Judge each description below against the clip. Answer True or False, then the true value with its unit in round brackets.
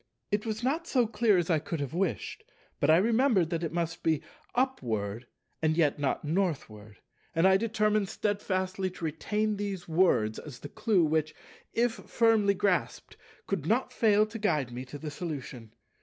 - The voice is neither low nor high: True (180 Hz)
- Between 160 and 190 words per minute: True (170 wpm)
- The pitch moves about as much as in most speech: False (5.9 semitones)